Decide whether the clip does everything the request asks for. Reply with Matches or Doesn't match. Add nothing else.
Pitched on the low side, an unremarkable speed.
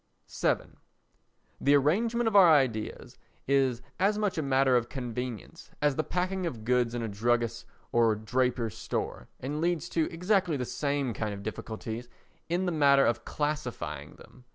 Matches